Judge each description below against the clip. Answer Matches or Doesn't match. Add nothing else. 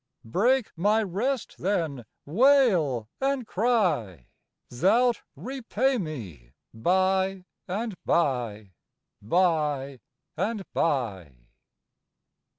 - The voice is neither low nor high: Matches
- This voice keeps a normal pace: Doesn't match